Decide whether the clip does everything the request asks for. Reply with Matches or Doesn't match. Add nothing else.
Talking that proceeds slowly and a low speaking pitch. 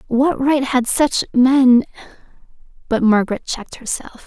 Doesn't match